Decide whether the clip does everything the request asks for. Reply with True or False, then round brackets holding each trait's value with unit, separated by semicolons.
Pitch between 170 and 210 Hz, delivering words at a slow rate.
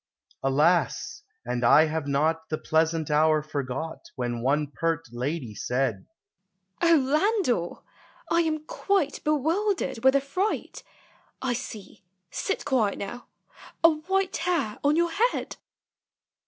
True (190 Hz; 130 wpm)